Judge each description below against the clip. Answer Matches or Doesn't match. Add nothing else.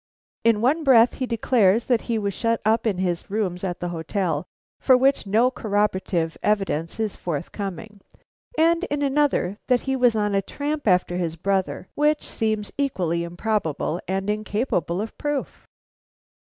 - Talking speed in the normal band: Matches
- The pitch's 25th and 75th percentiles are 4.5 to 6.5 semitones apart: Matches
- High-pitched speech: Matches